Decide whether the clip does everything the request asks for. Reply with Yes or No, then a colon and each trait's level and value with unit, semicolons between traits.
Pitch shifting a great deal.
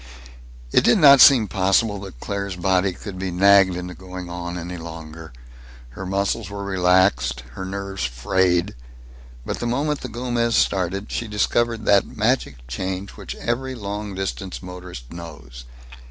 No: average, 2.9 semitones